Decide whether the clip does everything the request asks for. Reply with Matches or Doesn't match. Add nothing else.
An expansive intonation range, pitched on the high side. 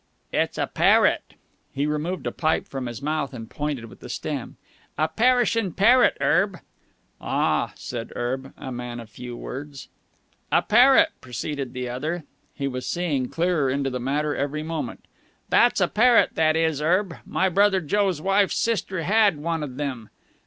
Doesn't match